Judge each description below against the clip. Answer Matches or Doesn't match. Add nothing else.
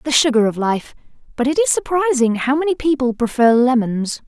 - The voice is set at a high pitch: Matches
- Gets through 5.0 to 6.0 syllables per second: Matches